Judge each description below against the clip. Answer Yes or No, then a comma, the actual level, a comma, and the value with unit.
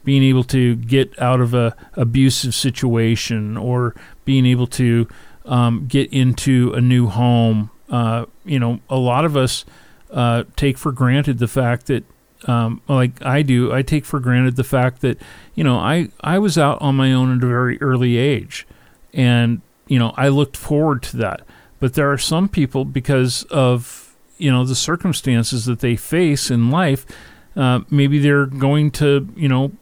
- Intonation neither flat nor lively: No, narrow, 2.3 semitones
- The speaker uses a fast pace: No, average, 180 wpm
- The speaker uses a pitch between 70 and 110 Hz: No, low, 130 Hz